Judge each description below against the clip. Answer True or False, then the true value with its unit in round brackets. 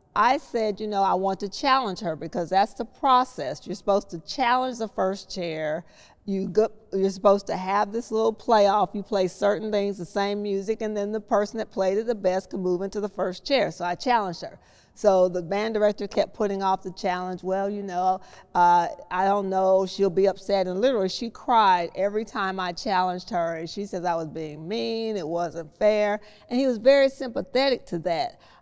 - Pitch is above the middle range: True (200 Hz)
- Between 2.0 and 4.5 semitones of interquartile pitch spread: True (2.9 semitones)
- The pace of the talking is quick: True (210 wpm)